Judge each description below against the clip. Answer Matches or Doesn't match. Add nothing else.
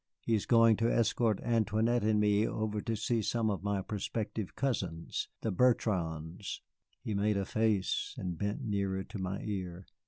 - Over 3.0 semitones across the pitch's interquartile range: Doesn't match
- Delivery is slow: Doesn't match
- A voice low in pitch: Matches